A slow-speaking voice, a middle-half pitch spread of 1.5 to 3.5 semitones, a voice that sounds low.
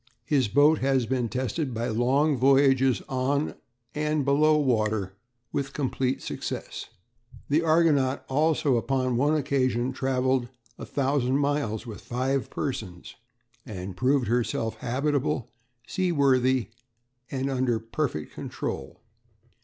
Yes: slow, 115 wpm; average, 2.8 semitones; low, 130 Hz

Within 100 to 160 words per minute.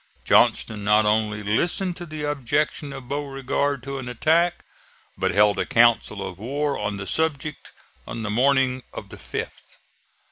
Yes: average, 155 wpm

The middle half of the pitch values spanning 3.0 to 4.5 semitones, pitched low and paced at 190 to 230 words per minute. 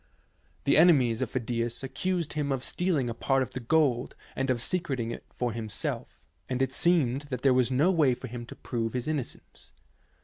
Yes: average, 3.8 semitones; low, 130 Hz; average, 200 wpm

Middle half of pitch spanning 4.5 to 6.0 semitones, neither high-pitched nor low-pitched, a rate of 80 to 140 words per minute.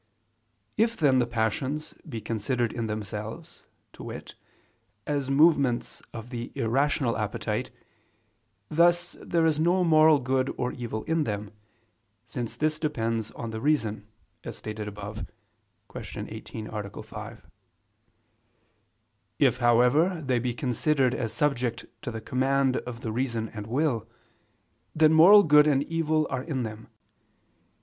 No: average, 5.0 semitones; low, 125 Hz; slow, 135 wpm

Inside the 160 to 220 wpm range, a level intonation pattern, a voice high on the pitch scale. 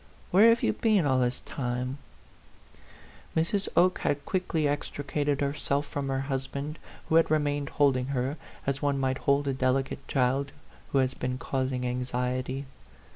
No: average, 180 wpm; narrow, 2.1 semitones; medium, 140 Hz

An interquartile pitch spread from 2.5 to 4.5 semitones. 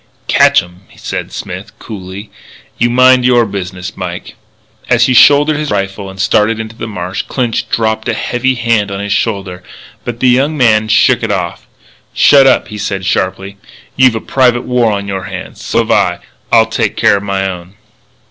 Yes: average, 3.9 semitones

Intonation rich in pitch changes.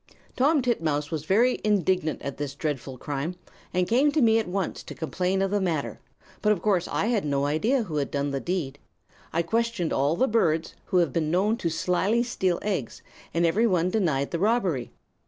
Yes: wide, 5.8 semitones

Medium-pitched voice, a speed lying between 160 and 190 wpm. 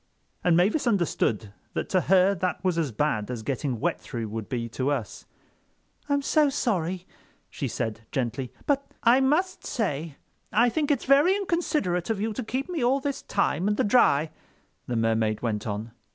Yes: medium, 180 Hz; average, 180 wpm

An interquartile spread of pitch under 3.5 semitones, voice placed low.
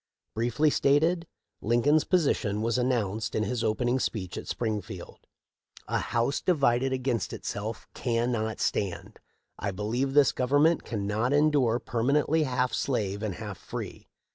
No: average, 4.2 semitones; low, 120 Hz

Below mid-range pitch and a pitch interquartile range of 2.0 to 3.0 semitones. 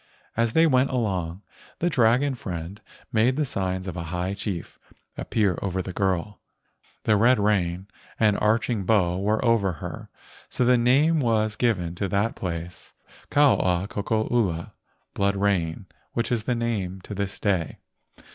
No: low, 100 Hz; average, 4.0 semitones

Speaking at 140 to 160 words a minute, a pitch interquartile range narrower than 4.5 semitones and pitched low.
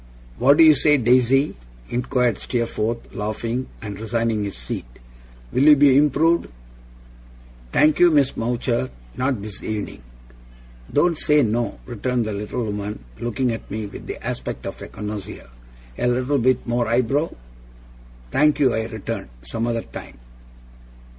Yes: average, 145 wpm; average, 3.8 semitones; low, 120 Hz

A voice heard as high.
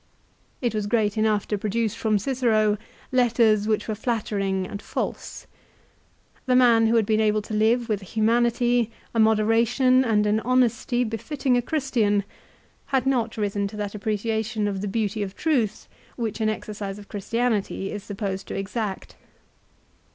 Yes: high, 220 Hz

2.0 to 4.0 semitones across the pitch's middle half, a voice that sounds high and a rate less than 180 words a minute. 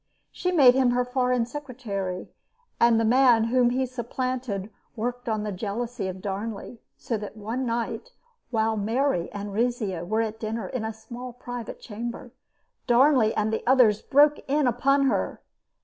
Yes: average, 2.7 semitones; high, 235 Hz; average, 160 wpm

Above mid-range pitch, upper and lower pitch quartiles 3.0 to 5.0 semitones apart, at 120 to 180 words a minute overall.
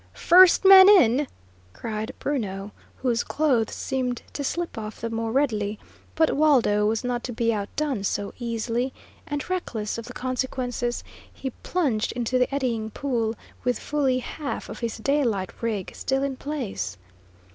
Yes: high, 245 Hz; average, 4.0 semitones; average, 150 wpm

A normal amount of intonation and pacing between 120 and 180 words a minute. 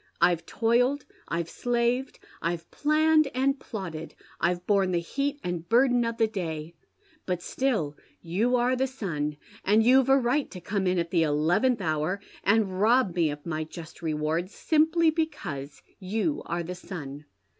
No: wide, 7.1 semitones; average, 160 wpm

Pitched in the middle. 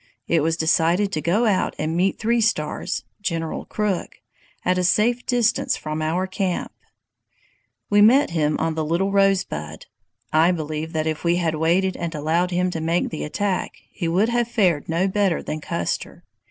Yes: medium, 175 Hz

